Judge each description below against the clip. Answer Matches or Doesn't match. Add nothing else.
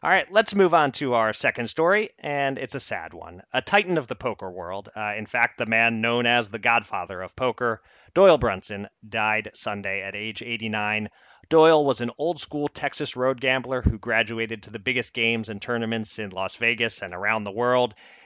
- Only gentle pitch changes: Doesn't match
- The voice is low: Matches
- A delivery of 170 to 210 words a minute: Matches